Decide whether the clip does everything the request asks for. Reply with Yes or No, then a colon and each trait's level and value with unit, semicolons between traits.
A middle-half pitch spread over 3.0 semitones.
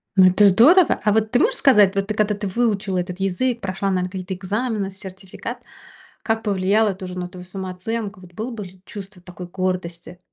No: average, 2.7 semitones